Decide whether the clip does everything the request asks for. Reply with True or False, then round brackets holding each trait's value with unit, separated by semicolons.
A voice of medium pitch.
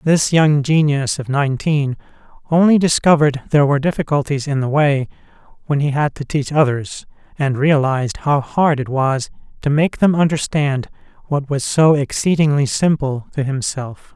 True (145 Hz)